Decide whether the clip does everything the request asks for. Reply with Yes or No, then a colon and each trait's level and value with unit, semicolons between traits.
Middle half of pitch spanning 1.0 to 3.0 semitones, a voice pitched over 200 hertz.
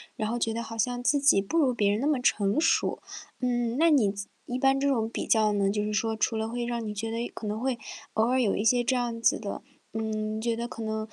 Yes: narrow, 2.4 semitones; high, 225 Hz